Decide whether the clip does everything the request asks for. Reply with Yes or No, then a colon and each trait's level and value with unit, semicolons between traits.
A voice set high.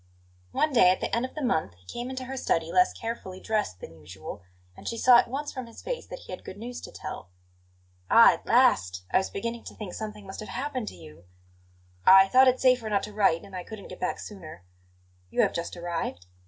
Yes: high, 210 Hz